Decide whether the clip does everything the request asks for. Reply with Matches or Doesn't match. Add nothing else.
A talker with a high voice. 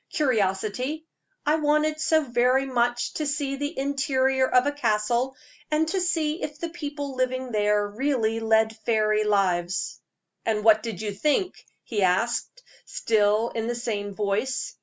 Matches